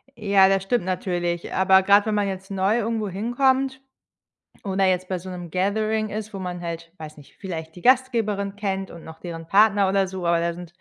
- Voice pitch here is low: No, high, 190 Hz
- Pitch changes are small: No, average, 3.0 semitones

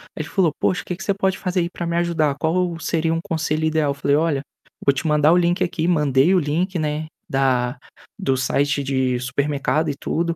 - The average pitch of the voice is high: No, medium, 155 Hz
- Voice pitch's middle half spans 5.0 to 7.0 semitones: No, average, 3.4 semitones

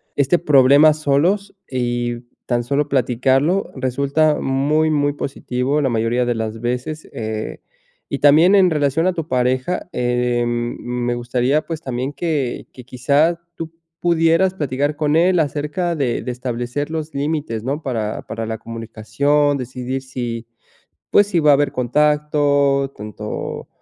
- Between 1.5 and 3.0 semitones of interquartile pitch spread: No, average, 3.8 semitones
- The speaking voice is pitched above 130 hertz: Yes, medium, 140 Hz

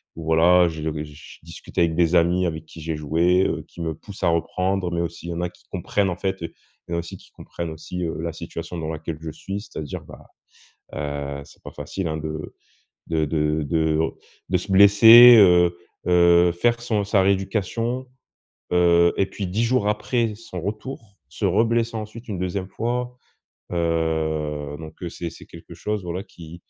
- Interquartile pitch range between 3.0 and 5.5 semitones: Yes, average, 3.6 semitones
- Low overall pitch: Yes, very low, 85 Hz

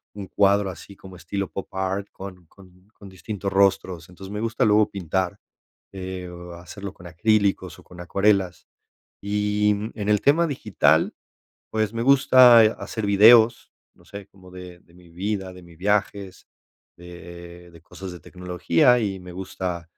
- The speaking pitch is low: Yes, very low, 95 Hz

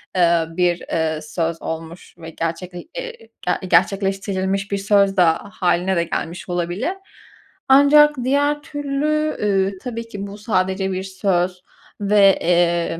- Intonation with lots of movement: No, average, 3.2 semitones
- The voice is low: No, high, 190 Hz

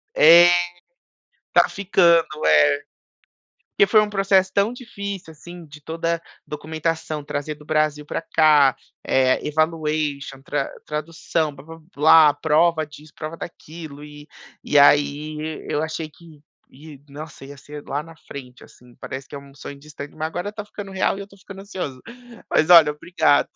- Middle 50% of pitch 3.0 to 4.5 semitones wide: No, narrow, 2.5 semitones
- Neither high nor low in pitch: Yes, medium, 155 Hz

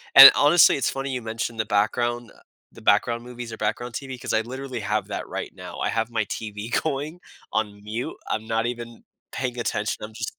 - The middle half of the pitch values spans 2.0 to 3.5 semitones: Yes, narrow, 2.4 semitones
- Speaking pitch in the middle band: No, low, 115 Hz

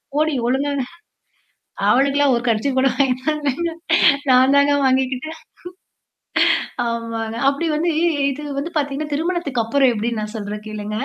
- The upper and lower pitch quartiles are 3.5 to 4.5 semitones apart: Yes, average, 3.8 semitones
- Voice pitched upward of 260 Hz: Yes, very high, 270 Hz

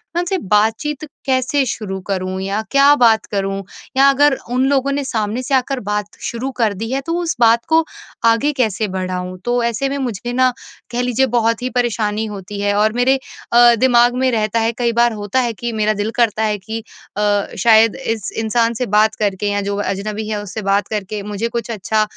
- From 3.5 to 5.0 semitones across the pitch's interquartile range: No, average, 3.1 semitones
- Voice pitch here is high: Yes, high, 225 Hz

